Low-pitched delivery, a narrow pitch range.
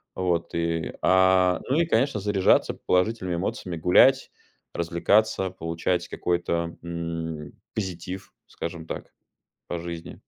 Yes: very low, 90 Hz; narrow, 2.1 semitones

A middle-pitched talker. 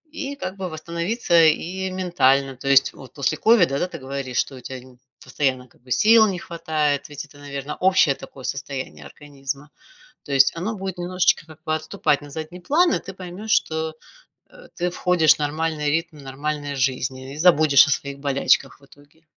Yes: medium, 150 Hz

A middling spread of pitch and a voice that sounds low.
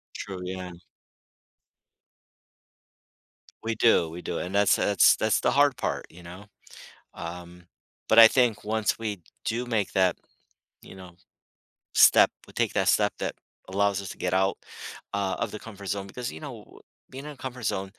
Yes: average, 3.5 semitones; low, 100 Hz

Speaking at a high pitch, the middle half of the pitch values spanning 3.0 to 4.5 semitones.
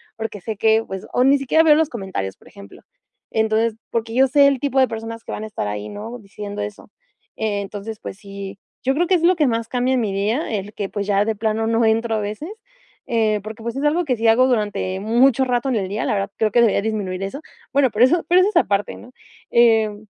Yes: high, 225 Hz; average, 3.6 semitones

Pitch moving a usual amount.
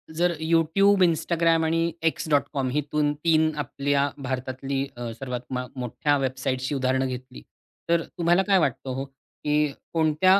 Yes: average, 3.8 semitones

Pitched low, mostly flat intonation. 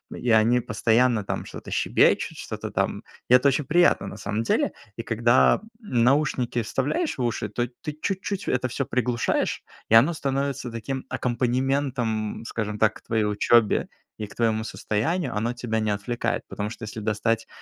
No: low, 120 Hz; average, 3.2 semitones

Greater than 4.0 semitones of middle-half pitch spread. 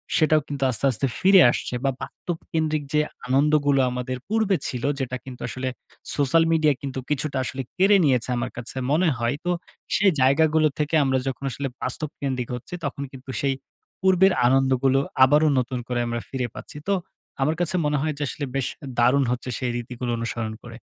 No: average, 3.4 semitones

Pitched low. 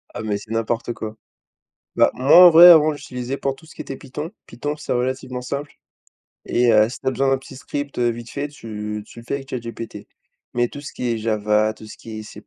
Yes: low, 125 Hz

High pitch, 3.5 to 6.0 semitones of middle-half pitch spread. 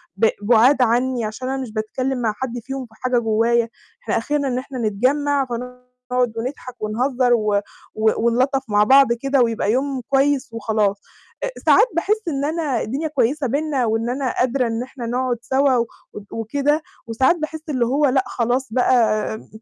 No: very high, 250 Hz; average, 2.9 semitones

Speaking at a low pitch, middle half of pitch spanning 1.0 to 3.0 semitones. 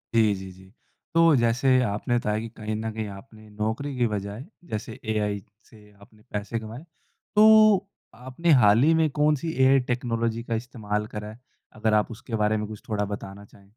No: low, 110 Hz; average, 3.4 semitones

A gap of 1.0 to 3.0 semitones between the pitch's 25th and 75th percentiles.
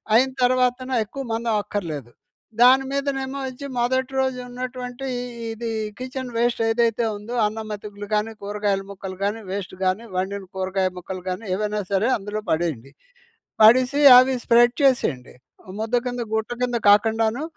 No: average, 3.9 semitones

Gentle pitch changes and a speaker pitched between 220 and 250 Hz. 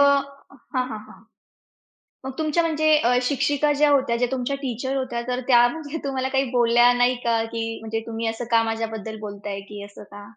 No: average, 3.4 semitones; high, 245 Hz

